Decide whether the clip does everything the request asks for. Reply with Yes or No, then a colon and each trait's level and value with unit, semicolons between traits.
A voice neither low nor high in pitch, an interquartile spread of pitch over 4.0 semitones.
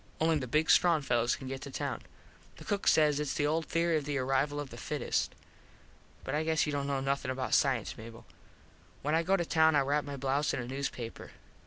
No: medium, 145 Hz; average, 2.7 semitones